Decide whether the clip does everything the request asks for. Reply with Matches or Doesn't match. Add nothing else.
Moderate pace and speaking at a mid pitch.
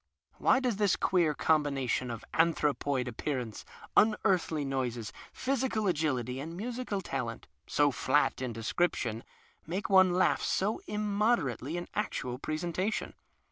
Doesn't match